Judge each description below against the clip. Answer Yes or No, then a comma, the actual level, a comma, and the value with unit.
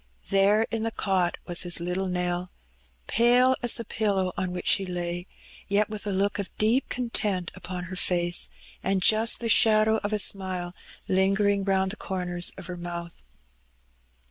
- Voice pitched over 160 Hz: Yes, high, 190 Hz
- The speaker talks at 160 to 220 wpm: Yes, average, 170 wpm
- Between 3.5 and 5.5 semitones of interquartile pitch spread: No, average, 3.0 semitones